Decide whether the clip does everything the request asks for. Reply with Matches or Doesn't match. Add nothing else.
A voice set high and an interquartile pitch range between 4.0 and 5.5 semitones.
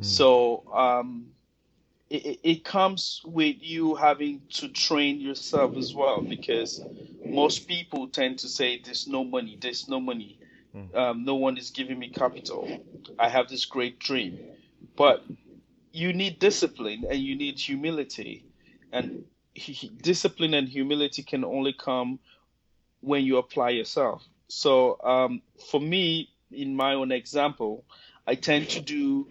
Doesn't match